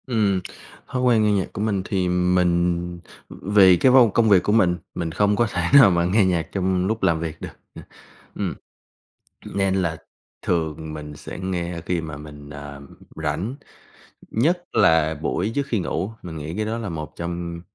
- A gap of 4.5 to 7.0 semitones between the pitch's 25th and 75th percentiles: No, average, 4.0 semitones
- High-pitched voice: No, very low, 90 Hz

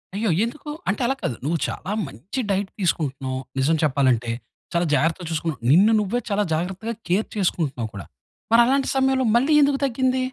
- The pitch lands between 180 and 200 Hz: Yes, high, 190 Hz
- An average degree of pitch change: No, wide, 8.0 semitones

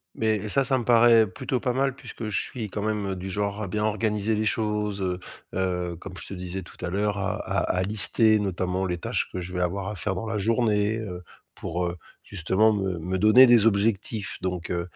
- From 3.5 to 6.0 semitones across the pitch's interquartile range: No, average, 2.9 semitones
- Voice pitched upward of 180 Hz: No, low, 100 Hz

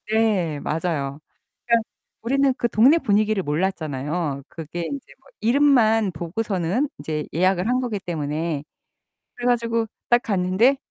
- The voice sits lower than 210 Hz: Yes, high, 195 Hz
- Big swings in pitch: Yes, wide, 6.3 semitones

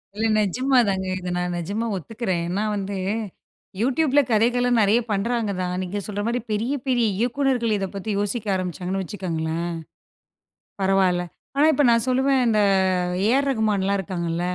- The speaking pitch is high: Yes, high, 205 Hz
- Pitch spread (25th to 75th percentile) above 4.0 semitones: Yes, average, 4.4 semitones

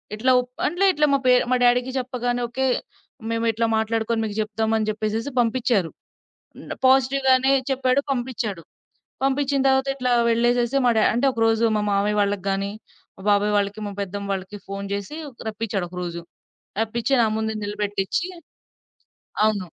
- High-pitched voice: Yes, high, 225 Hz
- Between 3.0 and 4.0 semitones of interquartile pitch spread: Yes, average, 3.7 semitones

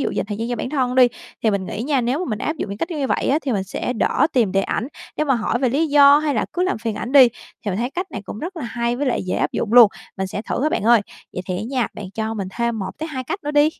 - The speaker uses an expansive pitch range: No, average, 4.8 semitones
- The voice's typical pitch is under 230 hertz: No, high, 245 Hz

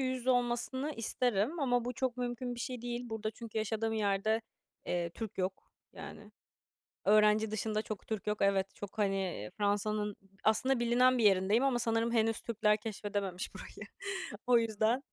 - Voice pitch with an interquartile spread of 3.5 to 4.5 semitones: No, average, 2.7 semitones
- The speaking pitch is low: No, high, 220 Hz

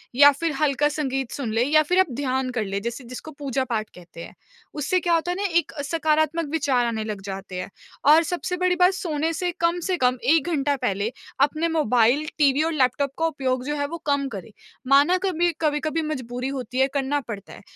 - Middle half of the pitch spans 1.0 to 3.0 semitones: No, average, 4.3 semitones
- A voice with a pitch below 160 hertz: No, very high, 285 Hz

